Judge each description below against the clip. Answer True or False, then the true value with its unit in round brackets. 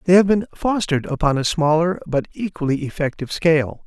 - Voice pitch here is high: False (160 Hz)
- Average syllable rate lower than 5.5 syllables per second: False (6.0 syllables/s)